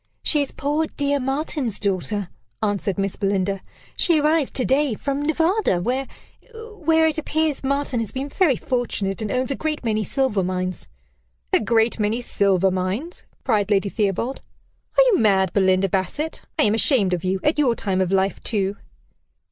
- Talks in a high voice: Yes, high, 230 Hz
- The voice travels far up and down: Yes, wide, 6.7 semitones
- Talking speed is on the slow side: No, average, 170 wpm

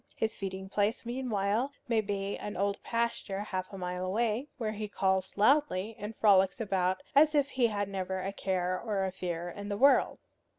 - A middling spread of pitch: Yes, average, 3.1 semitones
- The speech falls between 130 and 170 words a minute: No, average, 185 wpm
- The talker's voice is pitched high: Yes, high, 200 Hz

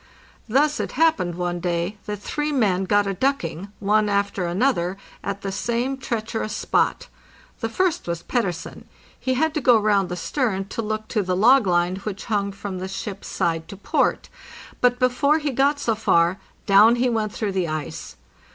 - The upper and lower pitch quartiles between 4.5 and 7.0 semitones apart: Yes, average, 4.8 semitones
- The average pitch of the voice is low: No, high, 210 Hz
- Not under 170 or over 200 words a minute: Yes, average, 180 wpm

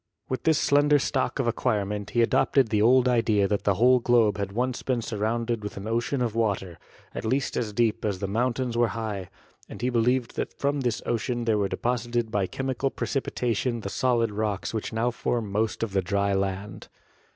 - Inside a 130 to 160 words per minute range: No, fast, 205 wpm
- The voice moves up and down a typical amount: Yes, average, 3.1 semitones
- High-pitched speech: No, low, 115 Hz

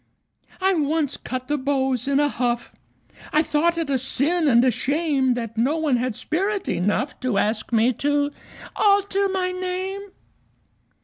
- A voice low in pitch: No, very high, 285 Hz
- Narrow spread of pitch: No, average, 5.1 semitones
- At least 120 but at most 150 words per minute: No, average, 160 wpm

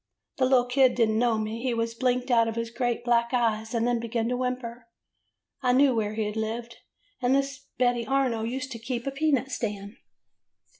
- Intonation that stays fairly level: Yes, narrow, 1.9 semitones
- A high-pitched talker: Yes, high, 240 Hz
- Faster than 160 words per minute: Yes, average, 200 wpm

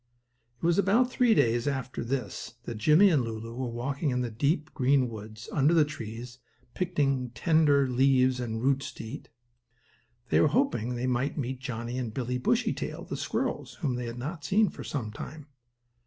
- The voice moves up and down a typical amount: Yes, average, 3.8 semitones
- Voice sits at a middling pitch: No, low, 130 Hz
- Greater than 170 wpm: Yes, average, 180 wpm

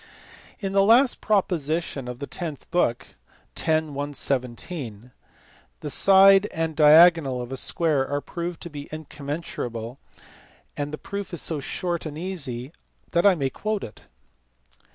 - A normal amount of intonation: Yes, average, 4.4 semitones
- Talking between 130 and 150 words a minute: Yes, slow, 135 wpm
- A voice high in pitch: No, medium, 155 Hz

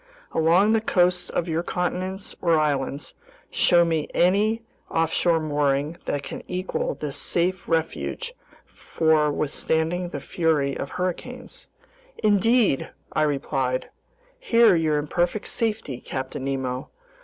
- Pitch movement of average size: Yes, average, 3.9 semitones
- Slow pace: Yes, slow, 120 wpm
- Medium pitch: Yes, medium, 165 Hz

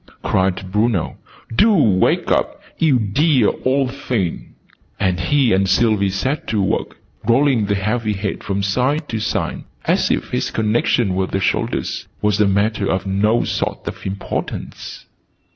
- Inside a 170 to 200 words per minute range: No, average, 150 wpm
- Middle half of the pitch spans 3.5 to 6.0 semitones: Yes, average, 4.3 semitones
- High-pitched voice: No, low, 105 Hz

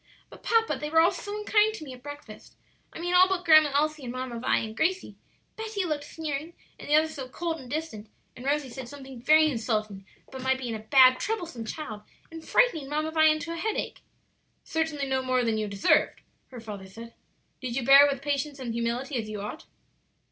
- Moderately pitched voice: No, very high, 285 Hz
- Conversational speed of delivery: No, fast, 215 wpm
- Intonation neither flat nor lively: Yes, average, 4.7 semitones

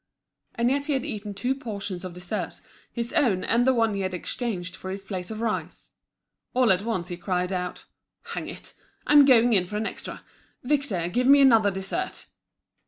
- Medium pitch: No, high, 215 Hz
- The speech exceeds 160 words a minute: Yes, average, 190 wpm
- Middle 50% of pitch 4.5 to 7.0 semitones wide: Yes, average, 5.0 semitones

